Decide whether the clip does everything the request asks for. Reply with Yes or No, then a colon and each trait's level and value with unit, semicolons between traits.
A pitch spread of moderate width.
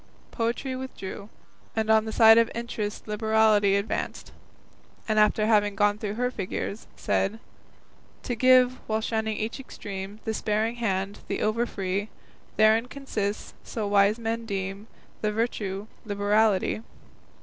No: narrow, 1.9 semitones